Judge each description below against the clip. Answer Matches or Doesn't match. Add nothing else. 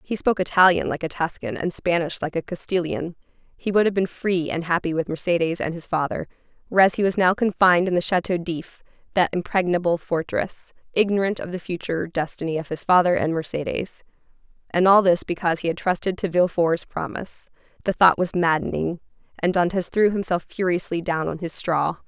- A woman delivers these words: Matches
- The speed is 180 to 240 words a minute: Matches